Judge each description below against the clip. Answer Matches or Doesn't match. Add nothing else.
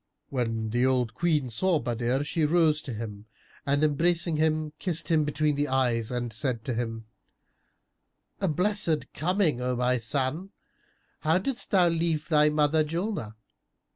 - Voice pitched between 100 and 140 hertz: Doesn't match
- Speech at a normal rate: Matches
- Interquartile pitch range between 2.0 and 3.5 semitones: Doesn't match